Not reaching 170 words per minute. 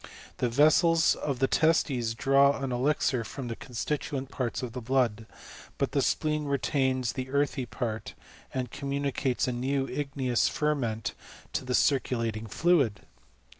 Yes: average, 140 wpm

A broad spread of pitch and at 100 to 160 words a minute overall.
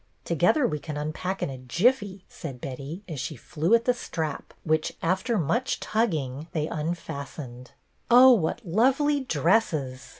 Yes: wide, 7.5 semitones; average, 155 wpm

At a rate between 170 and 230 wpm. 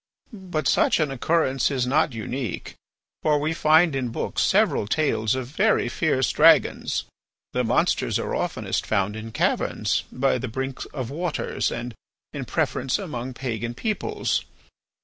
No: average, 145 wpm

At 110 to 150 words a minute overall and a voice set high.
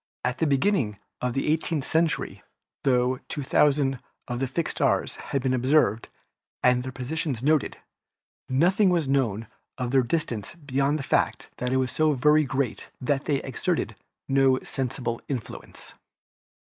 No: average, 145 wpm; low, 135 Hz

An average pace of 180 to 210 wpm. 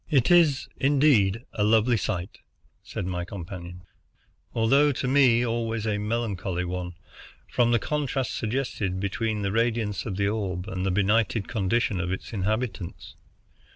No: average, 145 wpm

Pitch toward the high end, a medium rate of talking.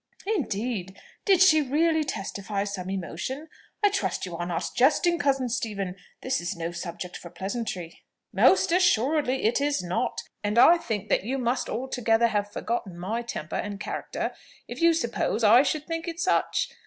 Yes: high, 235 Hz; average, 170 wpm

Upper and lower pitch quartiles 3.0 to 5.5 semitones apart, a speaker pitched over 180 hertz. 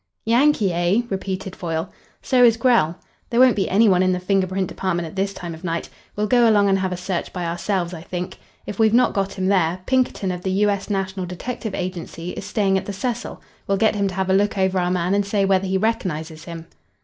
No: narrow, 2.4 semitones; high, 190 Hz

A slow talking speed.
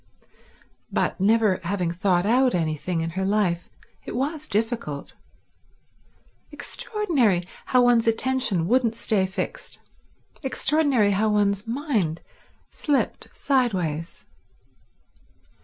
Yes: slow, 95 wpm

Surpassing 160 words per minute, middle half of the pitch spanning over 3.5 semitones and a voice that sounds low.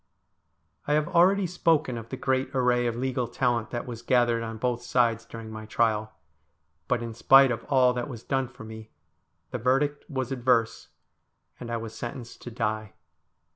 No: average, 175 wpm; narrow, 2.4 semitones; low, 120 Hz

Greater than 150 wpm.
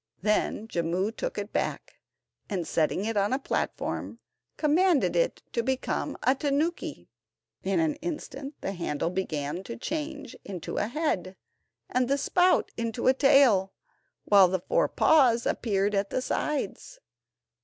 No: average, 145 wpm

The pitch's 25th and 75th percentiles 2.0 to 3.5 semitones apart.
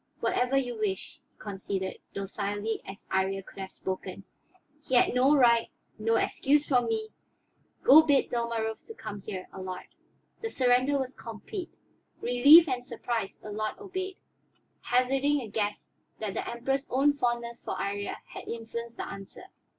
No: average, 4.5 semitones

